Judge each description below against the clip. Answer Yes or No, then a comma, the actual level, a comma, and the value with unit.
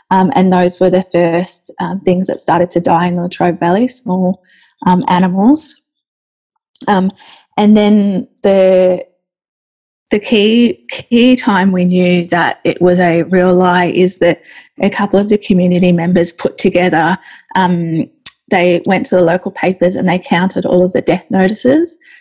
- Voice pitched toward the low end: No, medium, 185 Hz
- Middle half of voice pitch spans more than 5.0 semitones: No, narrow, 2.6 semitones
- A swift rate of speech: No, average, 160 wpm